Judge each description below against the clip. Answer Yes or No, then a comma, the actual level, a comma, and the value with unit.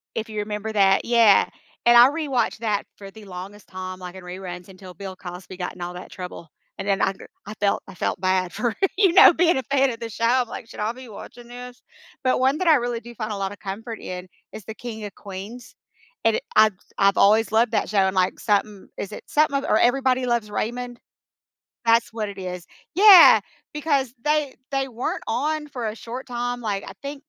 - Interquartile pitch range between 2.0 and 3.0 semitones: No, average, 4.2 semitones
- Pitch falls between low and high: No, high, 220 Hz